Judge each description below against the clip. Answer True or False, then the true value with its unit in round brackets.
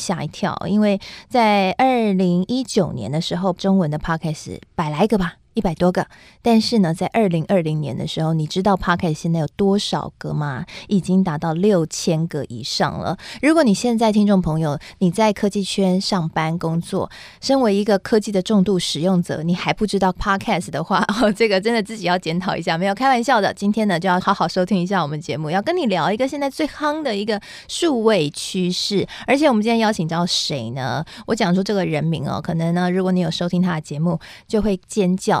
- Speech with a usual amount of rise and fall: True (4.0 semitones)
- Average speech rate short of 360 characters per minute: True (340 characters per minute)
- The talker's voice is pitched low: False (190 Hz)